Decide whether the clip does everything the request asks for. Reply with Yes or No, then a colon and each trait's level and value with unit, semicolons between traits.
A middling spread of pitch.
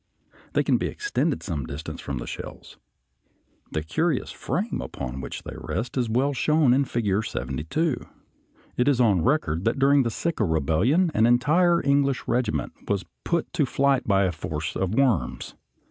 No: wide, 8.5 semitones